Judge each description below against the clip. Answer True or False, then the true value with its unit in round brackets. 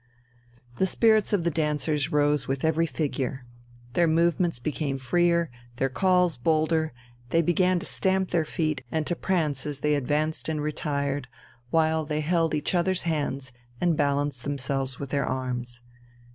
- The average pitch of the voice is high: False (155 Hz)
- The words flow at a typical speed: True (155 wpm)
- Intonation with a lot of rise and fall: False (3.2 semitones)